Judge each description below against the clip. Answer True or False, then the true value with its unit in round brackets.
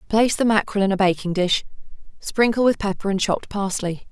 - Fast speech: False (190 wpm)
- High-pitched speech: True (200 Hz)